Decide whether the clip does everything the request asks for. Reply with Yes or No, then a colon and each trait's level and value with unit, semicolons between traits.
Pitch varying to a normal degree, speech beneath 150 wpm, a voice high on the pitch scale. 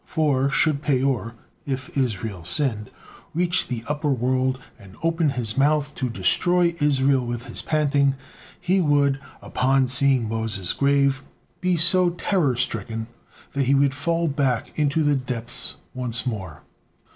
No: average, 3.6 semitones; average, 140 wpm; low, 135 Hz